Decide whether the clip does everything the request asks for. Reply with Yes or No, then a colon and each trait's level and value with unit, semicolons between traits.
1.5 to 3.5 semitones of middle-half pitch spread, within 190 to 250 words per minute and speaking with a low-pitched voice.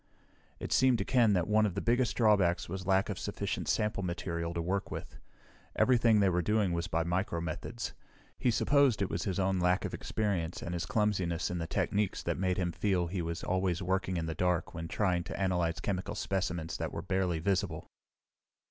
Yes: average, 3.0 semitones; average, 200 wpm; very low, 95 Hz